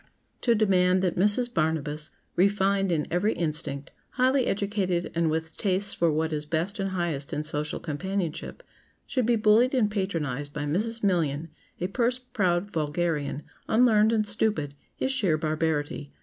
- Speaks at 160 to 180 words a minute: No, average, 150 wpm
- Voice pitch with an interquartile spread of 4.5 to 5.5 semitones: Yes, average, 5.2 semitones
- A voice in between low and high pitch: Yes, medium, 180 Hz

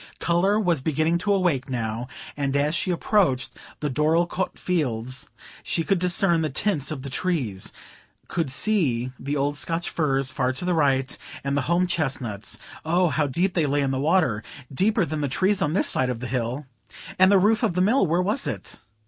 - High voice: No, medium, 155 Hz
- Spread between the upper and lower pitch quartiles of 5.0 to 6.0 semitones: Yes, average, 5.3 semitones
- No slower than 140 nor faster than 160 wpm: No, average, 180 wpm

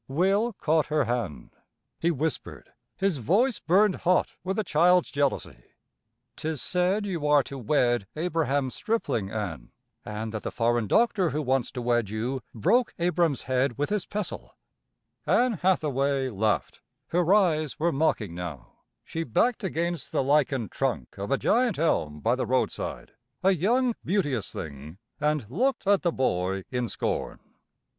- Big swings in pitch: Yes, wide, 7.2 semitones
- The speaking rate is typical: Yes, average, 150 wpm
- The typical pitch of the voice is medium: Yes, medium, 150 Hz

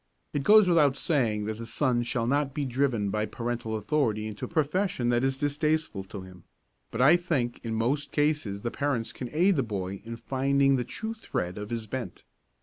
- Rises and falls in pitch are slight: No, average, 4.9 semitones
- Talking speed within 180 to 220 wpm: Yes, average, 200 wpm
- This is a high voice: No, low, 125 Hz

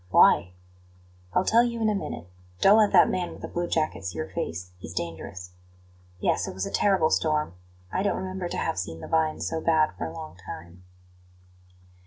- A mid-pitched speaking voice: Yes, medium, 155 Hz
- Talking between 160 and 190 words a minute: No, average, 200 wpm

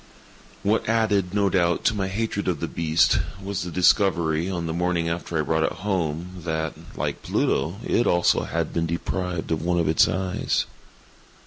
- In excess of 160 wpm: Yes, average, 180 wpm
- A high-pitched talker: No, very low, 90 Hz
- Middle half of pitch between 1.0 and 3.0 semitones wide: Yes, average, 2.7 semitones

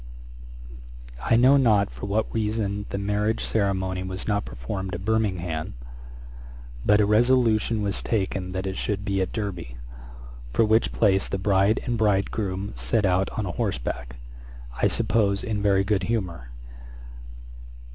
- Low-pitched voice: Yes, low, 100 Hz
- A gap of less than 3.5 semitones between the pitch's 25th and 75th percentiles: Yes, narrow, 2.6 semitones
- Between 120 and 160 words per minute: Yes, average, 145 wpm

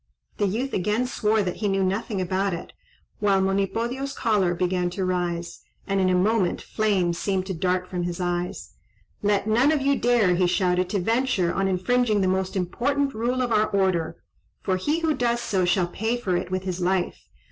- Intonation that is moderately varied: Yes, average, 3.8 semitones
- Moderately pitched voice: No, high, 195 Hz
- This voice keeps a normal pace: Yes, average, 195 wpm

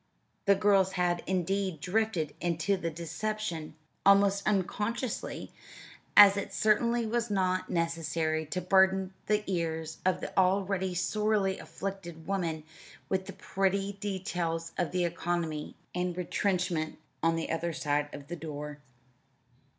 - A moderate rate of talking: No, slow, 125 wpm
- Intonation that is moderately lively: Yes, average, 3.2 semitones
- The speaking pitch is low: No, medium, 185 Hz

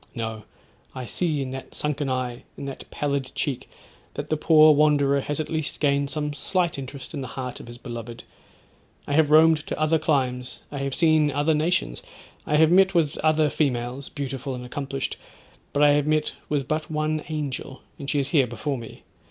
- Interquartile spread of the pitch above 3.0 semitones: No, average, 2.7 semitones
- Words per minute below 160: No, average, 195 wpm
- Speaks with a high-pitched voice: No, medium, 145 Hz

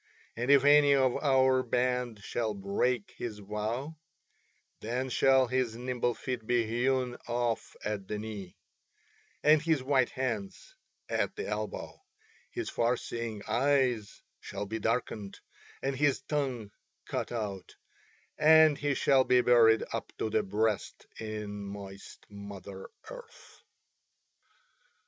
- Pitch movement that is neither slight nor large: Yes, average, 3.8 semitones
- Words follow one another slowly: Yes, slow, 125 wpm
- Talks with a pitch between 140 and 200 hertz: No, low, 120 Hz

